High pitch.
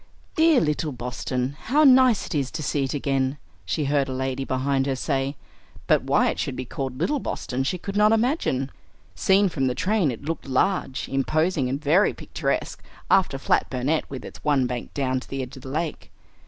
No: medium, 140 Hz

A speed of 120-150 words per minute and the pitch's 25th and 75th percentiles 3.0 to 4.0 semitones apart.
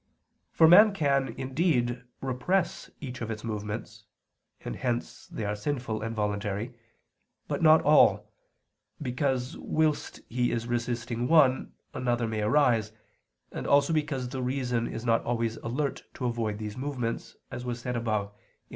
Yes: average, 145 wpm; average, 3.3 semitones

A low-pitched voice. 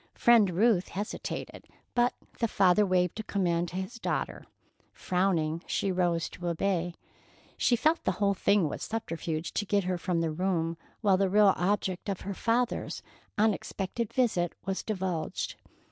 No: high, 190 Hz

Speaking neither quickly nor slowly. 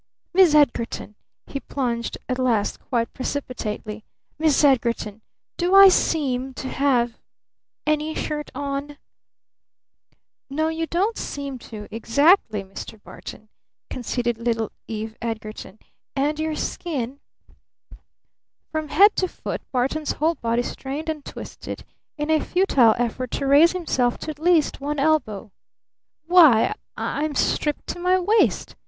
No: slow, 130 wpm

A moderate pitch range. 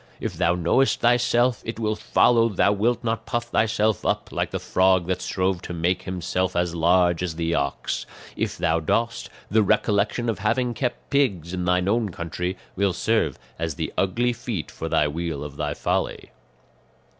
Yes: average, 5.0 semitones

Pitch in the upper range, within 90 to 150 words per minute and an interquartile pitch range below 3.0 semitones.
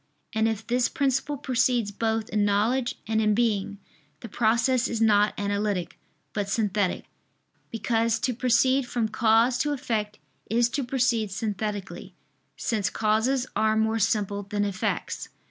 Yes: high, 220 Hz; average, 140 wpm; narrow, 2.6 semitones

